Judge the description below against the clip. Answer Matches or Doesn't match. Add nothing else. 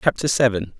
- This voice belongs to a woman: Doesn't match